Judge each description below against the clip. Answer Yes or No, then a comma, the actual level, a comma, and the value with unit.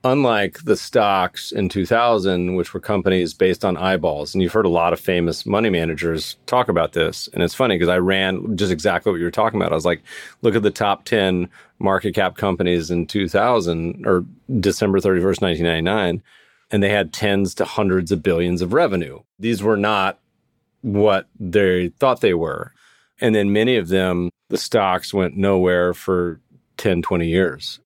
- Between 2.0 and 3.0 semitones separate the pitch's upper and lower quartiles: Yes, narrow, 2.4 semitones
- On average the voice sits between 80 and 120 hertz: Yes, very low, 95 Hz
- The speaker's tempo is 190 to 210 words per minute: No, average, 180 wpm